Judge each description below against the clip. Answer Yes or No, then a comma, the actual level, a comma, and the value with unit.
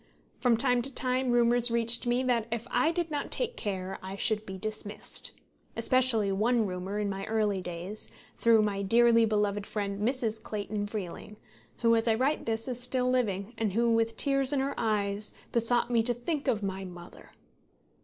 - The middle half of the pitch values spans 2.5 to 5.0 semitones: Yes, average, 3.1 semitones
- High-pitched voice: Yes, high, 225 Hz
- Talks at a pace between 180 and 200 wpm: Yes, average, 185 wpm